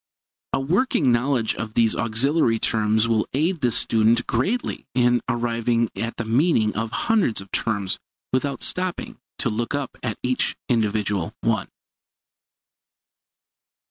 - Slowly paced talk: Yes, slow, 125 wpm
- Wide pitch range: No, average, 3.4 semitones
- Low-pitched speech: Yes, low, 115 Hz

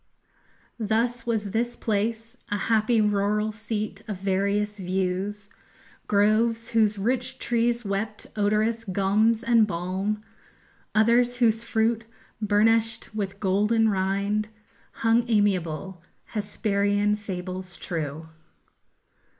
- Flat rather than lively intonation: Yes, narrow, 2.3 semitones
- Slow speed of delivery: Yes, slow, 100 wpm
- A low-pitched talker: No, high, 210 Hz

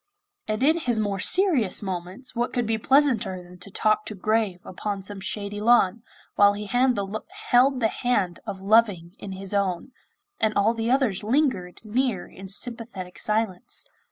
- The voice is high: Yes, high, 215 Hz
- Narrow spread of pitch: No, average, 3.8 semitones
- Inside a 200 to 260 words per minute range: No, average, 160 wpm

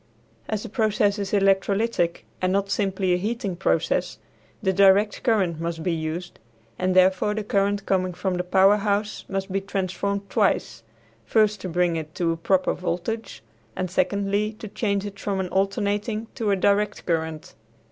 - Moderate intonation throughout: No, narrow, 2.1 semitones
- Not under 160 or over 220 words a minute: Yes, average, 170 wpm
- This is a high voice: Yes, high, 195 Hz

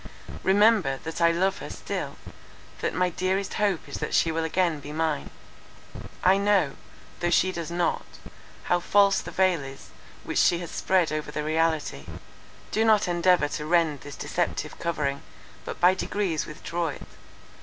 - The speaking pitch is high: No, medium, 170 Hz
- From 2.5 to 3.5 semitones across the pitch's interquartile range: Yes, average, 3.2 semitones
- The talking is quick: No, average, 160 wpm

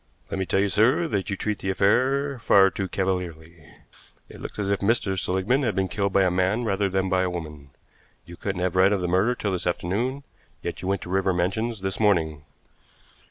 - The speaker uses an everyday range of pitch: No, narrow, 2.3 semitones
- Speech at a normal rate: No, fast, 215 wpm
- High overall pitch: No, very low, 95 Hz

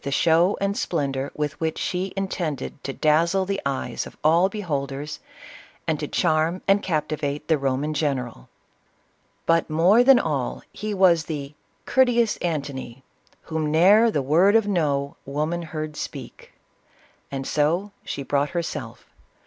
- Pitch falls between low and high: Yes, medium, 155 Hz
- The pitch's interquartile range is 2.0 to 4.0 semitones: No, average, 4.7 semitones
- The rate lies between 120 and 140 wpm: No, average, 155 wpm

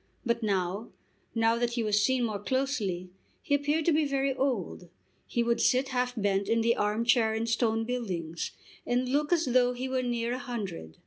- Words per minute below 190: No, average, 195 wpm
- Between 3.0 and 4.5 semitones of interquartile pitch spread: Yes, average, 3.4 semitones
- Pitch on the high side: Yes, high, 235 Hz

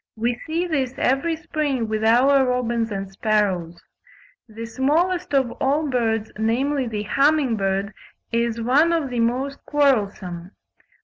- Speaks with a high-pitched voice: Yes, high, 245 Hz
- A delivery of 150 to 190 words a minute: No, slow, 135 wpm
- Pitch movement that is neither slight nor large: Yes, average, 4.3 semitones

